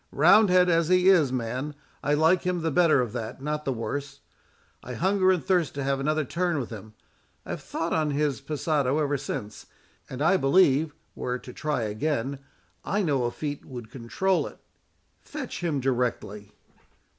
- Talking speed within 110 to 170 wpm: No, average, 180 wpm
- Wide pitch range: No, average, 4.8 semitones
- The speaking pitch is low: No, medium, 145 Hz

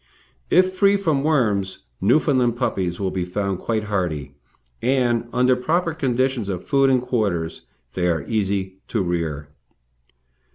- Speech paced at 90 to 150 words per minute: Yes, slow, 135 wpm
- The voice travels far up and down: Yes, wide, 6.1 semitones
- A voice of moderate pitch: No, low, 110 Hz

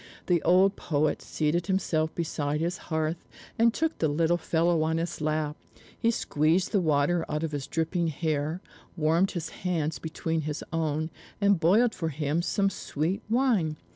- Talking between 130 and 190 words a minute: Yes, average, 165 wpm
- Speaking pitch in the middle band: Yes, medium, 165 Hz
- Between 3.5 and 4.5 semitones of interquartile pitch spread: No, narrow, 2.6 semitones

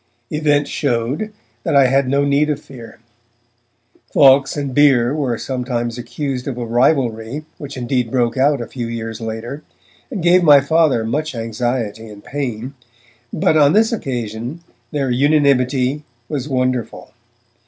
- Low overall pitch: Yes, low, 130 Hz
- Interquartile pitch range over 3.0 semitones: Yes, average, 3.4 semitones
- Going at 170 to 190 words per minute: No, average, 145 wpm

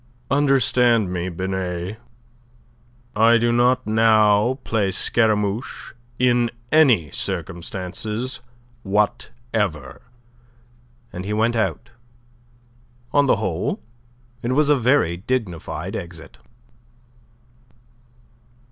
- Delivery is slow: Yes, slow, 85 wpm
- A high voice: No, low, 110 Hz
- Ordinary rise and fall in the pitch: Yes, average, 4.5 semitones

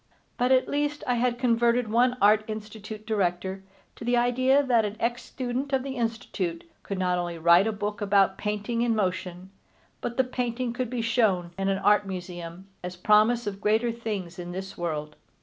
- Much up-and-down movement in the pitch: No, average, 4.2 semitones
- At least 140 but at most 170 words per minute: No, average, 185 wpm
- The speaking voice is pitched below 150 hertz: No, high, 215 Hz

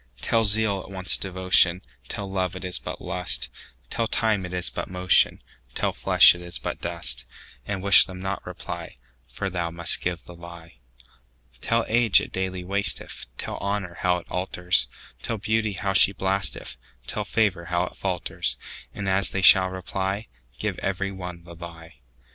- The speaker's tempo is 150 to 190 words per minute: No, average, 140 wpm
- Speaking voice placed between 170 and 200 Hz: No, very low, 90 Hz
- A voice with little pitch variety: Yes, narrow, 2.3 semitones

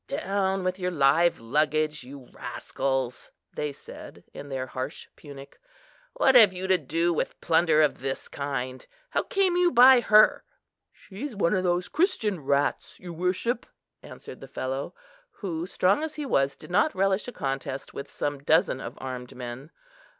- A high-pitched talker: No, medium, 165 Hz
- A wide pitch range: Yes, wide, 6.2 semitones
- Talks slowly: No, average, 165 wpm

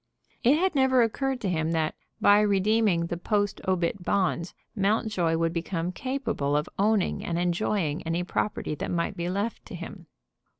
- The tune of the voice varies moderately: Yes, average, 4.3 semitones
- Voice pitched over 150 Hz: Yes, medium, 185 Hz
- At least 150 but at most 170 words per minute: Yes, average, 165 wpm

